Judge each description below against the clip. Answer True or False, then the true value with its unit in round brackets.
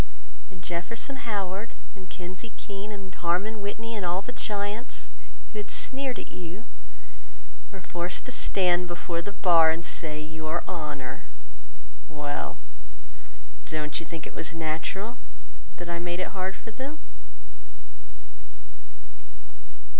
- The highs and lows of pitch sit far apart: False (3.6 semitones)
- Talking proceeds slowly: True (130 wpm)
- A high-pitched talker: False (180 Hz)